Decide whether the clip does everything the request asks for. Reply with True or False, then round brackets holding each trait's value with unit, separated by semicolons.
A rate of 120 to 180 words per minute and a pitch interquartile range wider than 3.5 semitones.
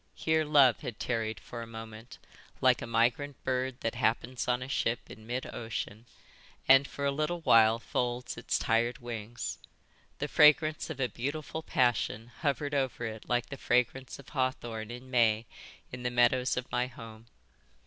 False (170 wpm; 2.7 semitones)